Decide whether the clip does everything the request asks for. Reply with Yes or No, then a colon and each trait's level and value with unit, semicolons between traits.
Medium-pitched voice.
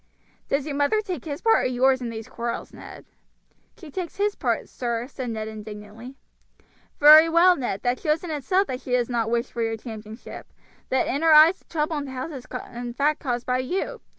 No: very high, 260 Hz